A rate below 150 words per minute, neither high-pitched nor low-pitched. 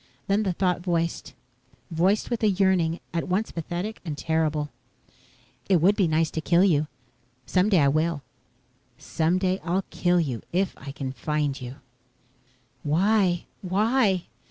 Yes: average, 140 wpm; medium, 175 Hz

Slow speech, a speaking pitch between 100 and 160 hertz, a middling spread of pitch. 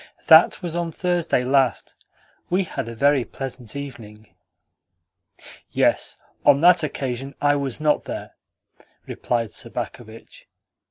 Yes: slow, 115 wpm; medium, 140 Hz; average, 4.7 semitones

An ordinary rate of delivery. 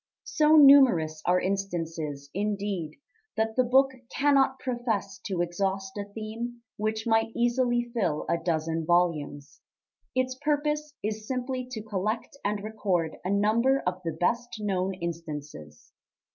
No: slow, 130 wpm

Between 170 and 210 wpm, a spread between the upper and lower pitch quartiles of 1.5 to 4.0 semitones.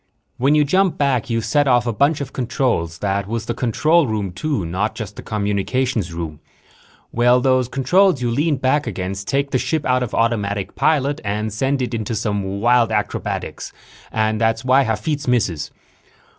No: average, 175 wpm; average, 4.5 semitones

